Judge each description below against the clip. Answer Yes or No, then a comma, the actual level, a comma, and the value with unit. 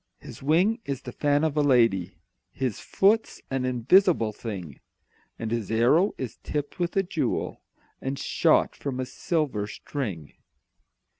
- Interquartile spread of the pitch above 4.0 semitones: Yes, wide, 5.5 semitones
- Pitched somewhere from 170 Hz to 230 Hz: No, low, 135 Hz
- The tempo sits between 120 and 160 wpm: Yes, average, 145 wpm